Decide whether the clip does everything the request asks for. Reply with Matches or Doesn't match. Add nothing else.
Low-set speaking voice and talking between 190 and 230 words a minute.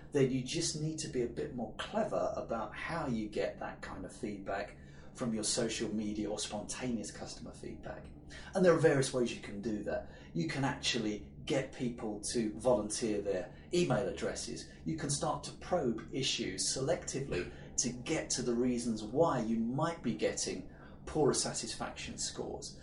Doesn't match